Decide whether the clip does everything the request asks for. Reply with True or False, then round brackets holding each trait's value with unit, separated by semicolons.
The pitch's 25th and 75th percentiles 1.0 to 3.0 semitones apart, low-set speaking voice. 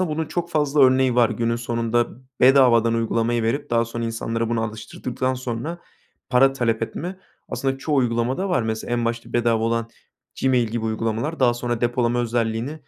True (2.4 semitones; 120 Hz)